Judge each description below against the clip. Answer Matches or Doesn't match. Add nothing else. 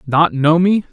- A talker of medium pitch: Matches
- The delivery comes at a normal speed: Matches